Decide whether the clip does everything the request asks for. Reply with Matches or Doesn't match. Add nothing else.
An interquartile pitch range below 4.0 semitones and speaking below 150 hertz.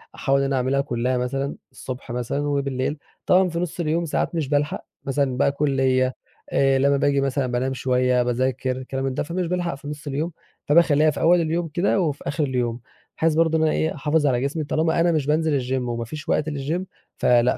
Matches